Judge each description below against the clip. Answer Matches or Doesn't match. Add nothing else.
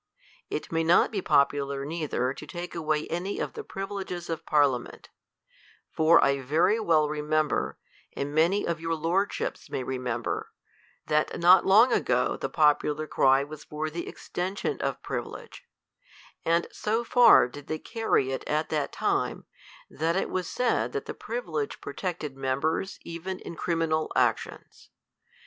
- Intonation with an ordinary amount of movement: Matches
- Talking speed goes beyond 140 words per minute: Matches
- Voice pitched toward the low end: Doesn't match